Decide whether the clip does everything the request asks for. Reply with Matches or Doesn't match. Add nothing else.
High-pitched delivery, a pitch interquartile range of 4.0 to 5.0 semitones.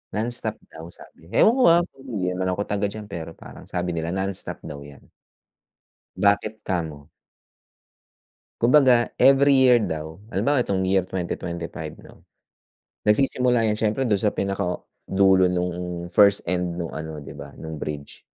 Doesn't match